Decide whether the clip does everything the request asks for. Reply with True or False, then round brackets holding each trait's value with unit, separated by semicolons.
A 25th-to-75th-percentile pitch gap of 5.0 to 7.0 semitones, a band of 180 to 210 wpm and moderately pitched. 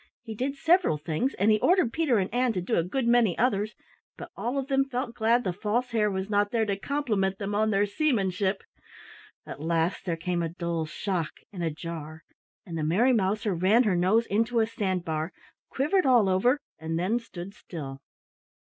False (5.4 semitones; 200 wpm; 205 Hz)